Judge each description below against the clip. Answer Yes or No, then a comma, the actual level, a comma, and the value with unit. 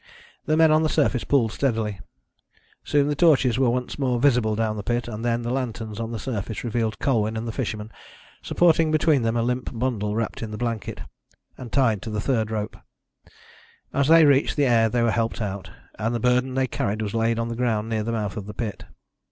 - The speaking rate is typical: No, fast, 215 wpm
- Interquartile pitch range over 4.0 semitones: No, average, 3.0 semitones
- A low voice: Yes, low, 115 Hz